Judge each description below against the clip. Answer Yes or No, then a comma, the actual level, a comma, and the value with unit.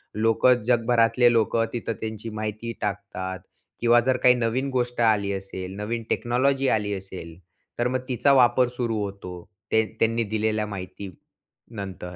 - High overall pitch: No, low, 115 Hz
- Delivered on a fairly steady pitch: No, average, 3.2 semitones